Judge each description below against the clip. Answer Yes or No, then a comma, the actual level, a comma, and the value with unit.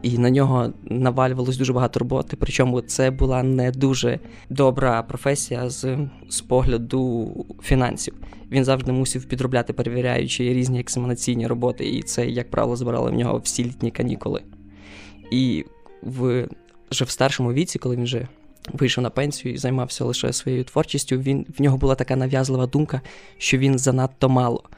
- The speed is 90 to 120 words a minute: No, fast, 155 wpm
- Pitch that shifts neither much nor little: No, narrow, 1.5 semitones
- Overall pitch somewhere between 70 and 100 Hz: No, low, 130 Hz